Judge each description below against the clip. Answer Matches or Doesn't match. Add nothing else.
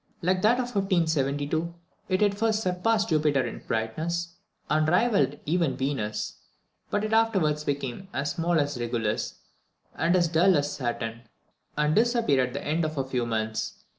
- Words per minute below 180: Matches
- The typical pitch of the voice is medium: Matches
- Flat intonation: Doesn't match